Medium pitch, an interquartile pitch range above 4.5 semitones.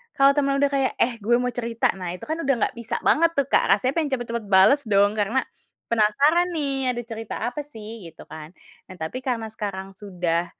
No: high, 230 Hz; wide, 5.4 semitones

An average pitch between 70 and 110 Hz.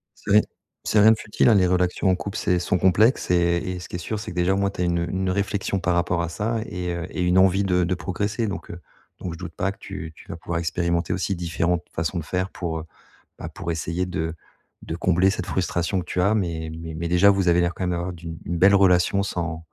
Yes: very low, 90 Hz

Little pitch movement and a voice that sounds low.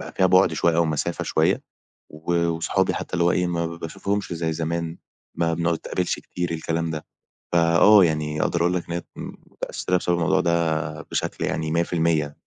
Yes: narrow, 1.2 semitones; very low, 85 Hz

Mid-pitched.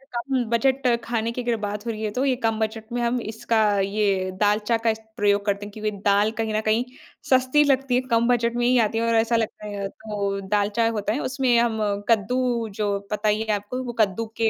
No: high, 225 Hz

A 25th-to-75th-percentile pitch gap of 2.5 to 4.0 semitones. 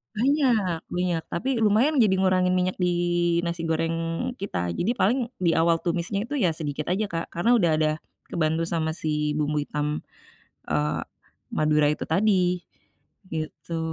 Yes: average, 3.5 semitones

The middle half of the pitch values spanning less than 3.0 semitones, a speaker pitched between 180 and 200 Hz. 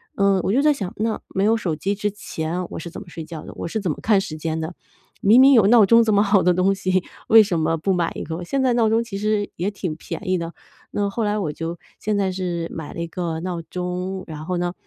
No: average, 3.7 semitones; medium, 185 Hz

